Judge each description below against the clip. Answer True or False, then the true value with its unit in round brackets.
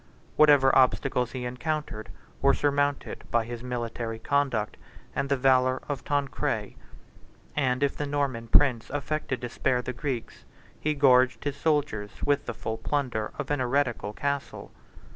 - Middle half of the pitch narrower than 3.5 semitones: True (2.9 semitones)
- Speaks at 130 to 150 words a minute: True (145 wpm)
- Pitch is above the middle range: False (130 Hz)